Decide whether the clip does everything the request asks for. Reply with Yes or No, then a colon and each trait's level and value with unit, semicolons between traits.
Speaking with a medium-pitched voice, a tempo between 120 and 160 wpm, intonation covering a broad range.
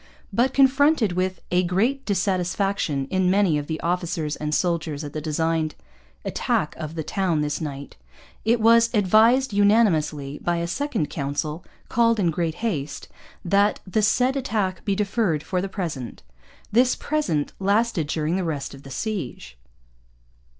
Yes: medium, 180 Hz; average, 150 wpm; wide, 5.8 semitones